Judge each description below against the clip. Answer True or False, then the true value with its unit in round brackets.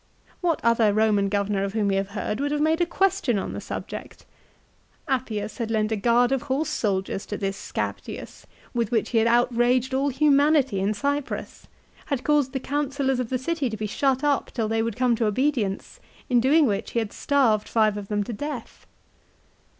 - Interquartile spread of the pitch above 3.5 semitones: True (4.7 semitones)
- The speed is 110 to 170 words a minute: False (200 wpm)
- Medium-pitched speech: False (240 Hz)